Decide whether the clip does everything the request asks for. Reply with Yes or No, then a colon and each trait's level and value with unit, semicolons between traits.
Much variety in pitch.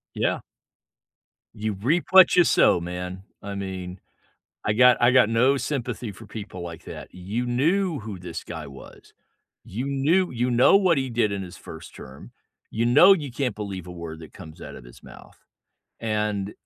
Yes: wide, 6.0 semitones